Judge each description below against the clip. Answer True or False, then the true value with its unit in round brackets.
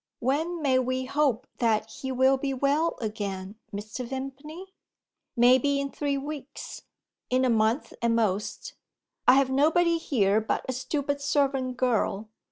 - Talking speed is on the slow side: False (145 wpm)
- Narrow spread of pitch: False (3.5 semitones)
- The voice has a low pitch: False (260 Hz)